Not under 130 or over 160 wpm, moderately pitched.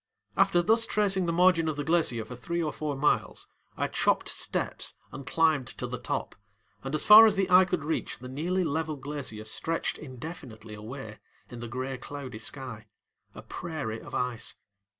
No: average, 180 wpm; medium, 145 Hz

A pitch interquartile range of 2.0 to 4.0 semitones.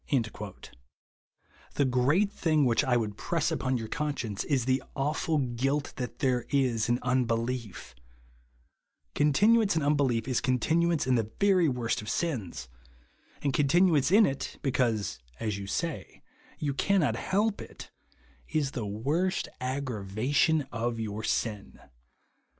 No: average, 4.8 semitones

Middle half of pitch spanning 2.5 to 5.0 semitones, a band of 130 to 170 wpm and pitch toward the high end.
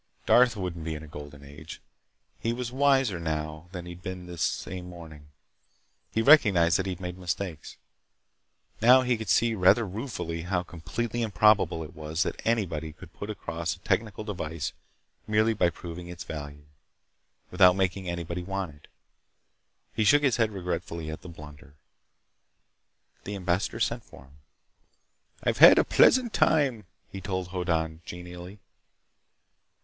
No: average, 4.5 semitones; average, 150 wpm; very low, 90 Hz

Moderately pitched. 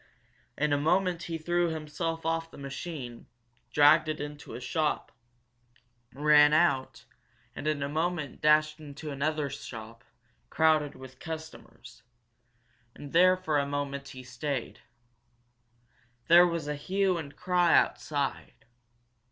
Yes: medium, 150 Hz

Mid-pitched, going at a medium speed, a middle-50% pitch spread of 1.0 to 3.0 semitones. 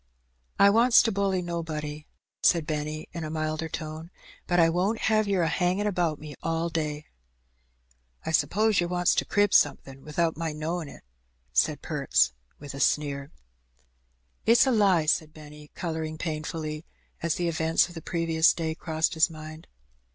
Yes: medium, 160 Hz; average, 165 wpm; narrow, 2.5 semitones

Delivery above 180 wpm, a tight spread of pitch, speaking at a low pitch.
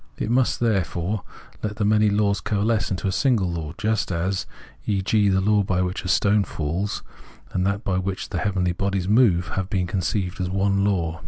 Yes: average, 190 wpm; narrow, 2.3 semitones; low, 100 Hz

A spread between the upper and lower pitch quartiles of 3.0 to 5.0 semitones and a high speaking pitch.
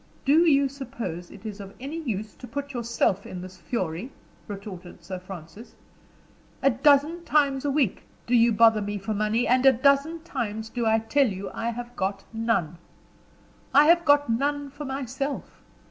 No: wide, 5.5 semitones; high, 235 Hz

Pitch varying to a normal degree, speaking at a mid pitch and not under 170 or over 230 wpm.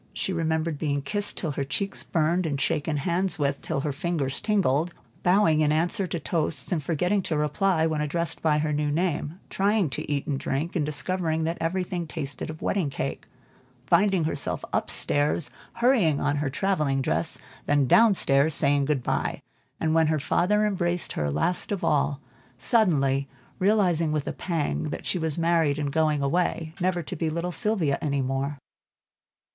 Yes: average, 3.6 semitones; medium, 160 Hz; average, 175 wpm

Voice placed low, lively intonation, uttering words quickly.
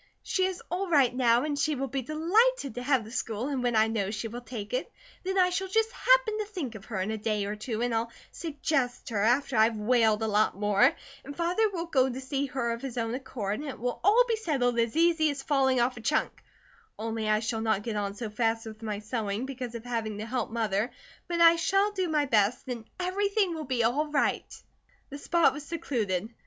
No: very high, 250 Hz; wide, 6.0 semitones; fast, 235 wpm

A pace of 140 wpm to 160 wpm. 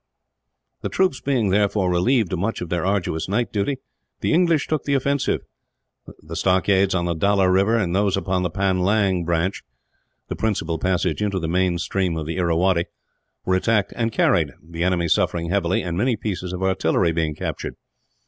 No: average, 175 wpm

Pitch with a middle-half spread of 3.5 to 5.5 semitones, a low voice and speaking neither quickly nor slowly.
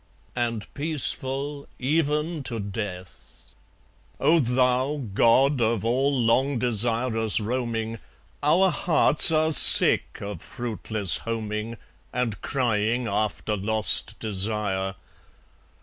No: average, 4.2 semitones; low, 115 Hz; slow, 95 wpm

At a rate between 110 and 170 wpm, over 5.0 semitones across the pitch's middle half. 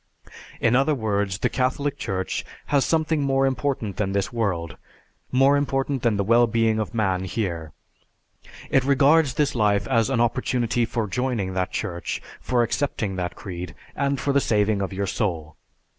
Yes: average, 165 wpm; wide, 5.5 semitones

